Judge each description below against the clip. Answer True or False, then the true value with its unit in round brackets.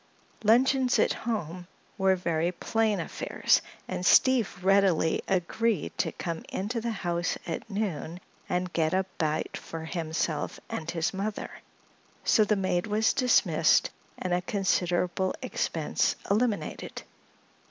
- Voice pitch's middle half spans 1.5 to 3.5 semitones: False (3.9 semitones)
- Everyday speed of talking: False (125 wpm)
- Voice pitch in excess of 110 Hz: True (185 Hz)